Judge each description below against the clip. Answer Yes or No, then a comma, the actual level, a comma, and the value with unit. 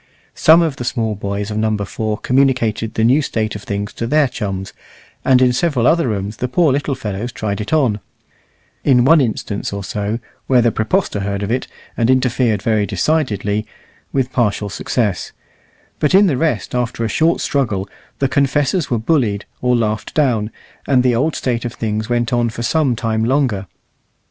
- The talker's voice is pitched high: No, low, 120 Hz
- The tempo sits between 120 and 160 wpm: No, average, 185 wpm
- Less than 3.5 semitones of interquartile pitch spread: No, average, 4.0 semitones